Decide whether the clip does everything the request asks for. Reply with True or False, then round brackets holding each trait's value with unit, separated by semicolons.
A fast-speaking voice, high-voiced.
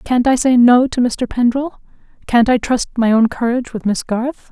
True (210 wpm; 240 Hz)